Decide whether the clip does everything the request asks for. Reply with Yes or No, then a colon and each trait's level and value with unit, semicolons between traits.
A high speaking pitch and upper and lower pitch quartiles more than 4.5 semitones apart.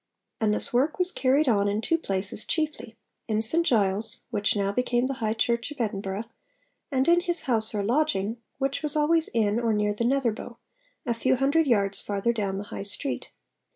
Yes: high, 235 Hz; average, 4.9 semitones